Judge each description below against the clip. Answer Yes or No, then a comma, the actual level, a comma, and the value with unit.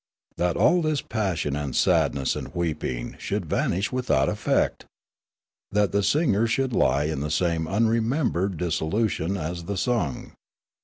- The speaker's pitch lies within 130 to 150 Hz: No, very low, 95 Hz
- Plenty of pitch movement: Yes, wide, 6.2 semitones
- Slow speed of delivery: No, average, 150 wpm